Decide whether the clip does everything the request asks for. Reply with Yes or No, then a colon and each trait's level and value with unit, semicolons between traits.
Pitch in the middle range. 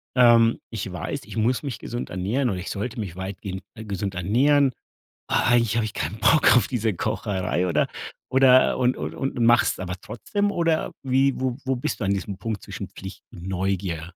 No: low, 110 Hz